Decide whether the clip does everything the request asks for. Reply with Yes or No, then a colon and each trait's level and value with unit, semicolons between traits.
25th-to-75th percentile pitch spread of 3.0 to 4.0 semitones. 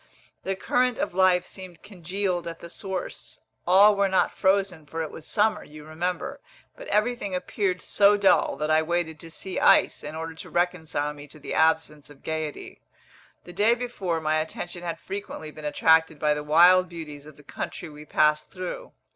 Yes: average, 3.5 semitones